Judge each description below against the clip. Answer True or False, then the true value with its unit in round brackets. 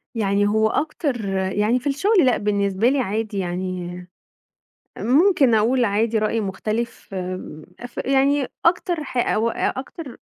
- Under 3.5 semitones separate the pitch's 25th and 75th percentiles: False (5.2 semitones)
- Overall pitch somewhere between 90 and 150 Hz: False (225 Hz)